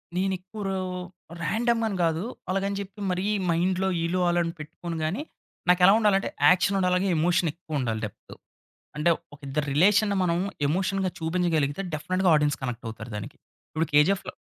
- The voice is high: No, medium, 180 Hz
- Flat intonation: No, average, 3.9 semitones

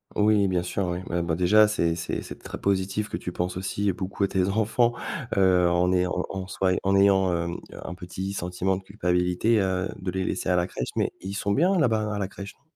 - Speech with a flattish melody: Yes, narrow, 2.0 semitones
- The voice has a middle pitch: No, very low, 95 Hz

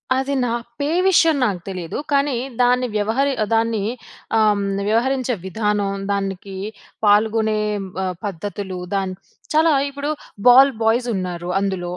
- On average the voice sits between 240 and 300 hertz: No, high, 215 Hz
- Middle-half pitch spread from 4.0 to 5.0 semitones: Yes, average, 4.6 semitones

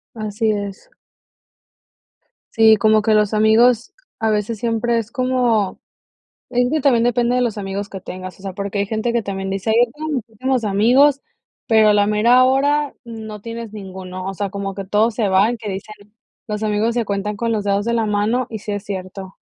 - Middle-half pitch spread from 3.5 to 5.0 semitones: No, average, 2.8 semitones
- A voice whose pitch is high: Yes, high, 215 Hz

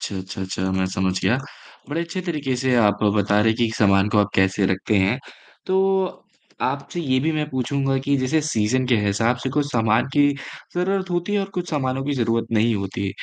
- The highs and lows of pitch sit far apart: Yes, wide, 6.4 semitones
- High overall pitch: No, low, 125 Hz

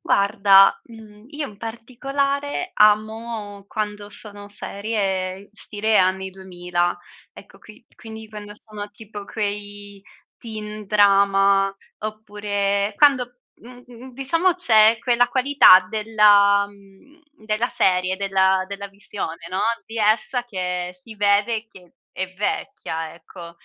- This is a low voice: No, high, 210 Hz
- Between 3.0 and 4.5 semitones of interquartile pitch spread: No, narrow, 2.4 semitones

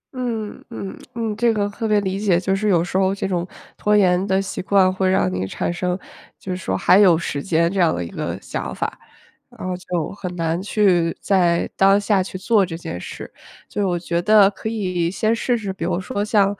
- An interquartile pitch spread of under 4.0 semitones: Yes, average, 2.8 semitones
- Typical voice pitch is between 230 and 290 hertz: No, high, 190 Hz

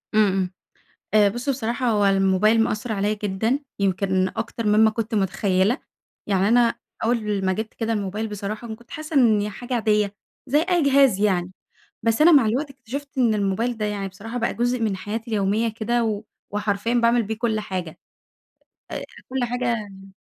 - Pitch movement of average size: Yes, average, 3.0 semitones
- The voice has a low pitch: No, high, 220 Hz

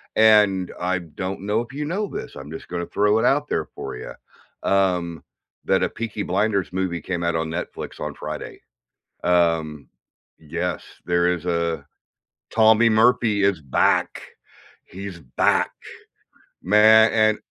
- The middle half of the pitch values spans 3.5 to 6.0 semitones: Yes, average, 4.2 semitones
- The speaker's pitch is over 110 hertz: No, very low, 95 Hz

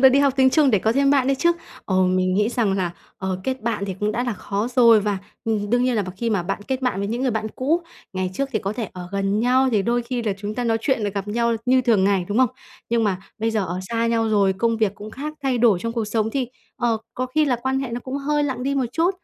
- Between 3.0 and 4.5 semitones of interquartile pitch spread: Yes, average, 4.0 semitones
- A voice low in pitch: No, high, 230 Hz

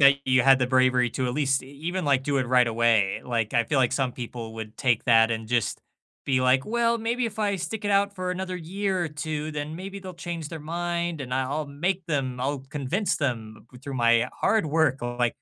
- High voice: No, medium, 140 Hz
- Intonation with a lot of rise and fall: Yes, wide, 5.7 semitones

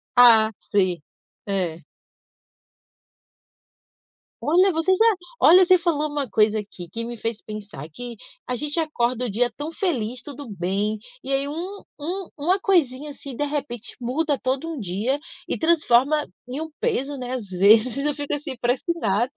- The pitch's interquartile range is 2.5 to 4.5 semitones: No, wide, 5.5 semitones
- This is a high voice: Yes, very high, 255 Hz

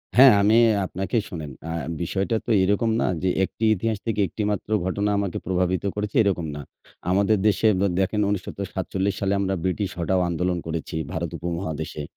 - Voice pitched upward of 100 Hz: No, very low, 95 Hz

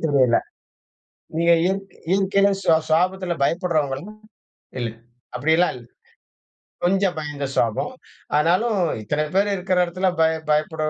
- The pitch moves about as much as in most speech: Yes, average, 4.0 semitones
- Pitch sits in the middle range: Yes, medium, 170 Hz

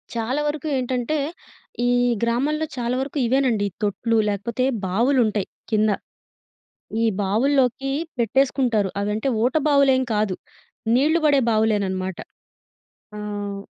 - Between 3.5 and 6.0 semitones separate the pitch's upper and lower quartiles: Yes, average, 4.4 semitones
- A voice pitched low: No, high, 235 Hz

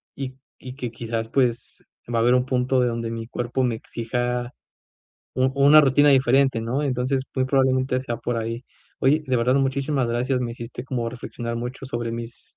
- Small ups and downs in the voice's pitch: Yes, narrow, 2.1 semitones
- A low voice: Yes, low, 125 Hz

